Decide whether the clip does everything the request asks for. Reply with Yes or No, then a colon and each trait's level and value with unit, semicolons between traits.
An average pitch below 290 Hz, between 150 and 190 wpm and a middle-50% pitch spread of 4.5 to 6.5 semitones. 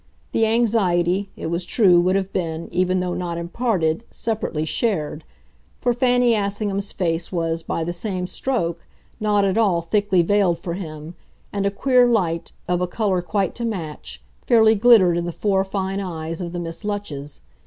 No: medium, 185 Hz; average, 175 wpm; average, 3.7 semitones